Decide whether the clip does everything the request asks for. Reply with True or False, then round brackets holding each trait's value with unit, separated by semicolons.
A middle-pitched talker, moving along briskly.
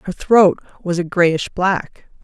False (180 Hz; 160 wpm)